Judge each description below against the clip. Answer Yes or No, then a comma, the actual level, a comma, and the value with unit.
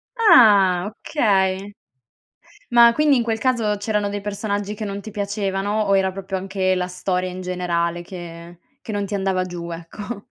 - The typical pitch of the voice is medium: No, high, 195 Hz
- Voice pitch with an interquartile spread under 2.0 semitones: No, narrow, 2.4 semitones